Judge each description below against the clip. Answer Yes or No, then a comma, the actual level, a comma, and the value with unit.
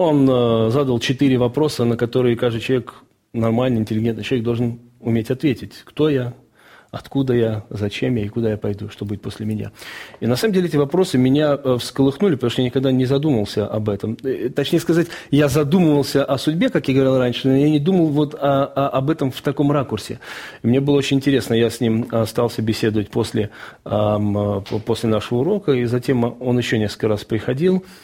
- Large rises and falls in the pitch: No, average, 3.8 semitones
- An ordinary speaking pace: No, fast, 185 wpm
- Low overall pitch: Yes, low, 125 Hz